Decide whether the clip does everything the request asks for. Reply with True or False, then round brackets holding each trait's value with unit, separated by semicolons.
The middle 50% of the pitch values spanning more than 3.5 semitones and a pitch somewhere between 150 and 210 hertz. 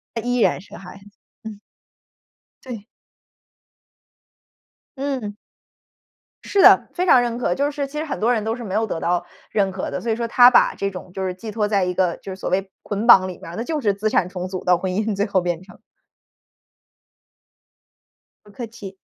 True (4.0 semitones; 205 Hz)